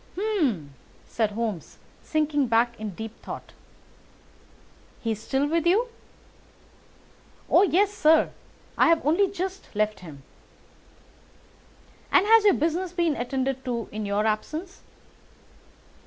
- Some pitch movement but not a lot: No, wide, 8.4 semitones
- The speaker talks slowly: Yes, slow, 120 wpm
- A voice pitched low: No, very high, 285 Hz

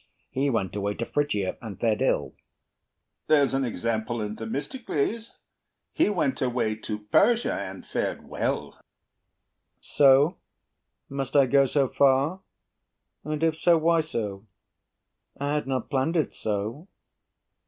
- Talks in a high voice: No, low, 135 Hz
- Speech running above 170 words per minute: No, slow, 135 wpm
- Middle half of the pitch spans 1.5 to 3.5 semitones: No, average, 5.3 semitones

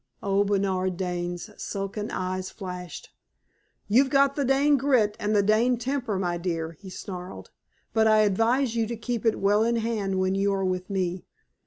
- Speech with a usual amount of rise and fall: Yes, average, 3.7 semitones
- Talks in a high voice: Yes, high, 205 Hz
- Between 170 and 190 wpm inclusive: Yes, average, 175 wpm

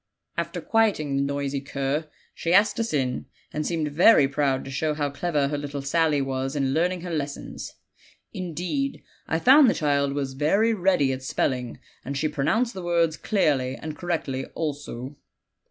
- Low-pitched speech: No, medium, 150 Hz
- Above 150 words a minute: Yes, average, 170 wpm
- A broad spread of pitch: No, average, 4.0 semitones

